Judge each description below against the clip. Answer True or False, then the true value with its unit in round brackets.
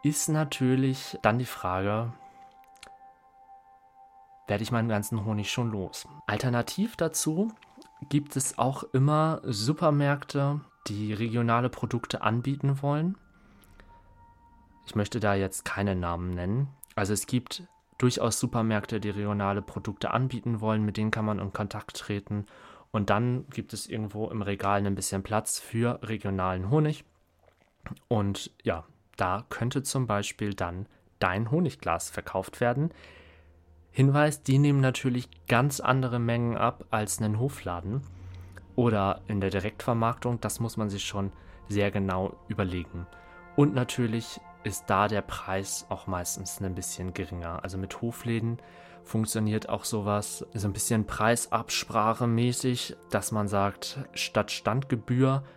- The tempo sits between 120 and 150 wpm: True (130 wpm)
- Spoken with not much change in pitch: False (4.8 semitones)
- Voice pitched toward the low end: True (110 Hz)